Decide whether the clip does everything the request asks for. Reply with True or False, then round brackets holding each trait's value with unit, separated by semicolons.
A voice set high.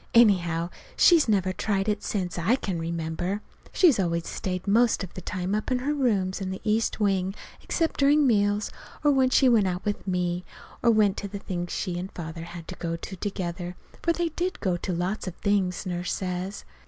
True (195 Hz)